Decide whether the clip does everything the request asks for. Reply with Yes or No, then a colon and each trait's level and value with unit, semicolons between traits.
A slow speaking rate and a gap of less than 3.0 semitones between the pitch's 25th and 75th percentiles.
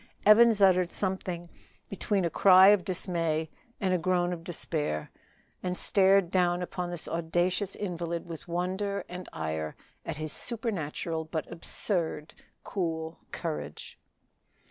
Yes: slow, 125 wpm; narrow, 2.6 semitones